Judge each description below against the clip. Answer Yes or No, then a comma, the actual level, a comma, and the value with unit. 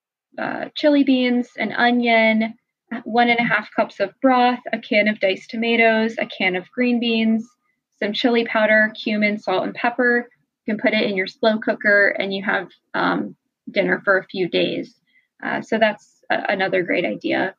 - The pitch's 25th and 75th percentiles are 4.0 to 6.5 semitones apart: No, average, 2.7 semitones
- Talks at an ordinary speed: Yes, average, 180 wpm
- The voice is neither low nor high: No, high, 225 Hz